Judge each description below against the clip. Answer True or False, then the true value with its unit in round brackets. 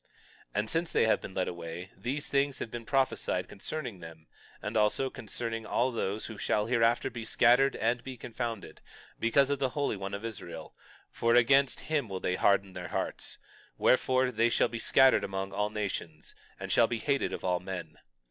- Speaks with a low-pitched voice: True (115 Hz)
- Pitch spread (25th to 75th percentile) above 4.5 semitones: True (4.9 semitones)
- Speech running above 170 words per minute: True (190 wpm)